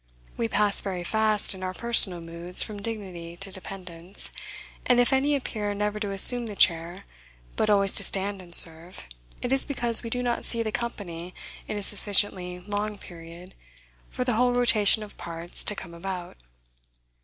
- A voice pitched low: No, high, 200 Hz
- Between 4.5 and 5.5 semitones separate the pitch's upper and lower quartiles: No, average, 3.7 semitones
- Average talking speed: Yes, average, 175 wpm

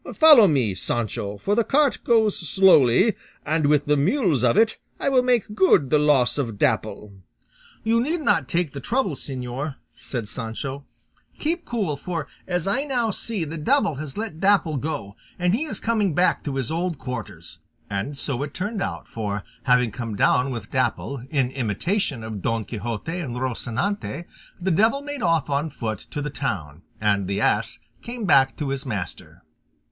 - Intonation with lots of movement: Yes, wide, 8.5 semitones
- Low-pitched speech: No, medium, 150 Hz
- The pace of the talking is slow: No, average, 175 wpm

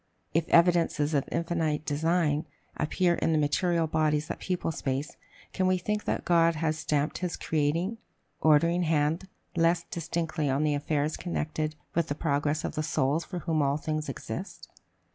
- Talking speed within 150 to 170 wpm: Yes, average, 160 wpm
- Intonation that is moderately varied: No, narrow, 2.2 semitones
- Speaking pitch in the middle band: Yes, medium, 160 Hz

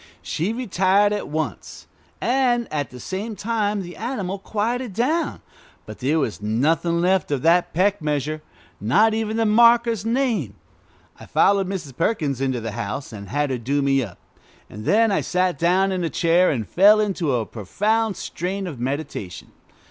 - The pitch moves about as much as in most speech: No, wide, 7.2 semitones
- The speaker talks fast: No, average, 170 wpm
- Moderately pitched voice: Yes, medium, 180 Hz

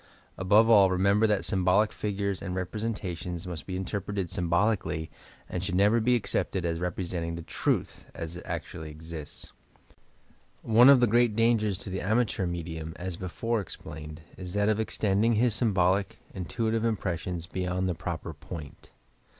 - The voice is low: Yes, very low, 95 Hz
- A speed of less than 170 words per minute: Yes, average, 160 wpm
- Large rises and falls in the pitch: No, average, 3.7 semitones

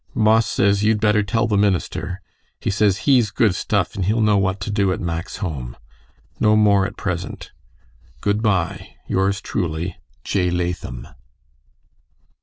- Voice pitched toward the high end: No, low, 100 Hz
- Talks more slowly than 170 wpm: Yes, average, 150 wpm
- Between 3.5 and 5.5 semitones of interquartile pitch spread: No, average, 2.8 semitones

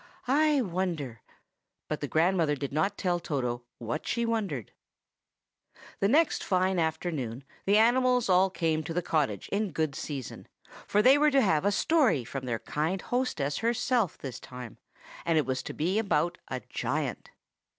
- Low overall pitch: No, medium, 170 Hz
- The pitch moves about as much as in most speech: No, wide, 6.9 semitones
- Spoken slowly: No, average, 160 wpm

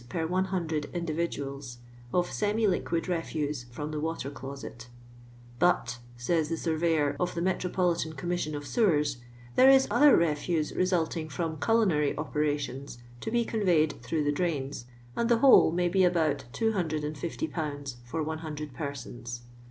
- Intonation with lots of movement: No, average, 3.6 semitones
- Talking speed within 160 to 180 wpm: No, average, 145 wpm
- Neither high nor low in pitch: Yes, medium, 160 Hz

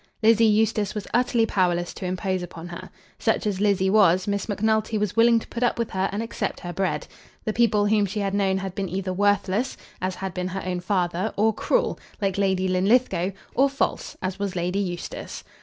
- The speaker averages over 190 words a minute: Yes, fast, 205 wpm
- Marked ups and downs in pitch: No, average, 2.7 semitones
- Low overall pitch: No, high, 195 Hz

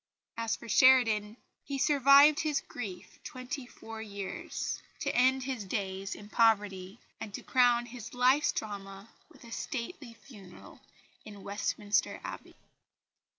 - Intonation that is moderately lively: Yes, average, 4.1 semitones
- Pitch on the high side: Yes, high, 230 Hz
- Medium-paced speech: No, slow, 130 wpm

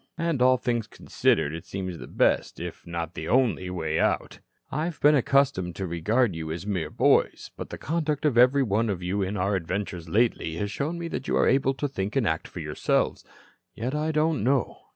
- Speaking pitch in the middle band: No, low, 110 Hz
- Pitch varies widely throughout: Yes, wide, 7.4 semitones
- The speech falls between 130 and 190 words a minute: No, fast, 205 wpm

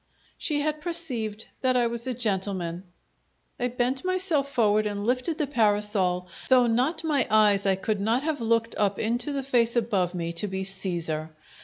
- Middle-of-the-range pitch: No, high, 230 Hz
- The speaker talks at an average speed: Yes, average, 175 wpm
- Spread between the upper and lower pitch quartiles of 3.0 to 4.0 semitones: No, average, 4.7 semitones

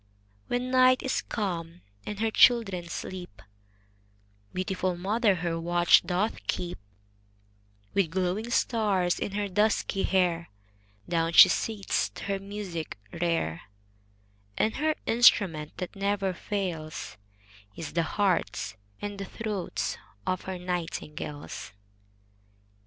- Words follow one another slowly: Yes, slow, 115 wpm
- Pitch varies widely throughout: No, average, 3.5 semitones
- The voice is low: No, medium, 185 Hz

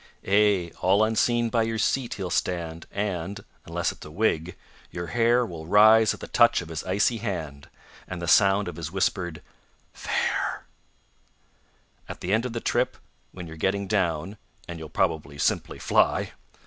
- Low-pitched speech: Yes, very low, 95 Hz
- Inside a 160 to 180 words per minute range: Yes, average, 165 wpm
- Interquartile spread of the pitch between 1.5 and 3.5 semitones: No, average, 4.5 semitones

